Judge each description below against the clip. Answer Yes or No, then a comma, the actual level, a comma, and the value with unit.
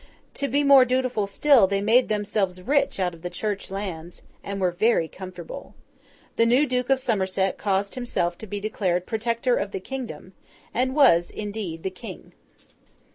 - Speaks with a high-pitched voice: Yes, high, 205 Hz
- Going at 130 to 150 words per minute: No, average, 170 wpm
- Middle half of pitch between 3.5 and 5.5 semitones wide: Yes, average, 5.0 semitones